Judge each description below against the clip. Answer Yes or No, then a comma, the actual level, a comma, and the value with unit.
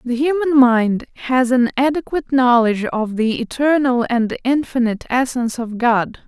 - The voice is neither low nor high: No, very high, 250 Hz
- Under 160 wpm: Yes, average, 145 wpm